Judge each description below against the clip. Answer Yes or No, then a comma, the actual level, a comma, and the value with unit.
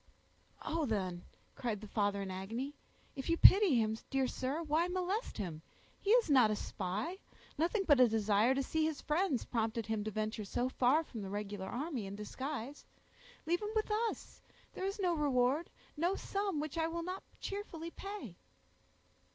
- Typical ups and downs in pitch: No, wide, 7.6 semitones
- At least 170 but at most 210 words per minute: Yes, average, 175 wpm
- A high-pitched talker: Yes, very high, 270 Hz